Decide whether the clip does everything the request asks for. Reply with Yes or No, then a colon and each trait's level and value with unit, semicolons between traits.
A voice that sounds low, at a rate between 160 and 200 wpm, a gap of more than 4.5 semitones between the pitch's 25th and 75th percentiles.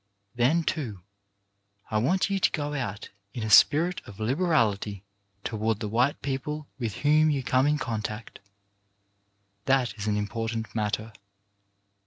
No: low, 120 Hz; average, 140 wpm; wide, 5.4 semitones